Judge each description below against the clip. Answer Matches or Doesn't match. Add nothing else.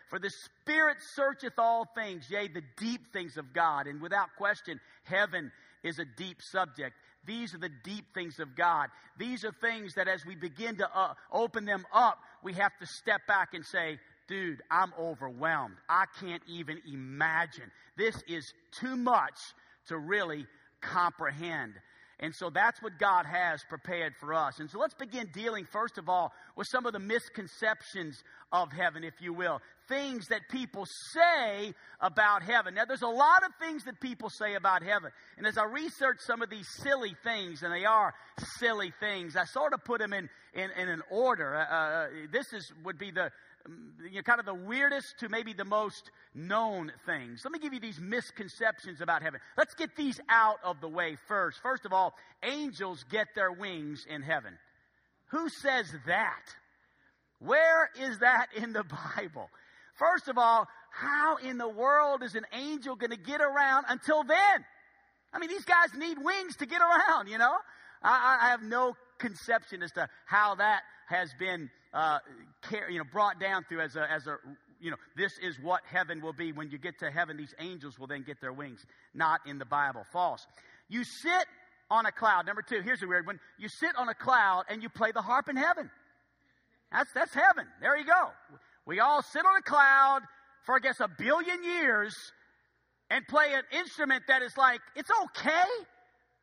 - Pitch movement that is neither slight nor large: Doesn't match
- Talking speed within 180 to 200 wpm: Matches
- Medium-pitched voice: Doesn't match